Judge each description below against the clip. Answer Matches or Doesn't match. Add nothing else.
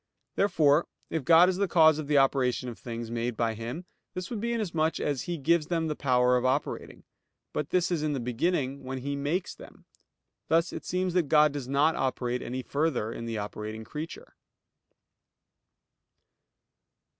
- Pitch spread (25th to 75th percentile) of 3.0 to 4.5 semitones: Doesn't match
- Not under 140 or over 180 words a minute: Matches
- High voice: Doesn't match